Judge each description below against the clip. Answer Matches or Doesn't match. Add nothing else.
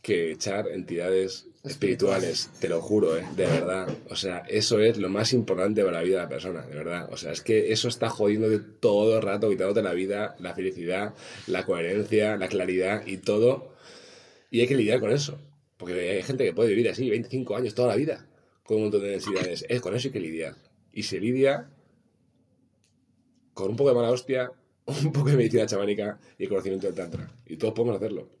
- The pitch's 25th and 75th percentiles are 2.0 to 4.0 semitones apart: Doesn't match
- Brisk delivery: Matches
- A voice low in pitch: Matches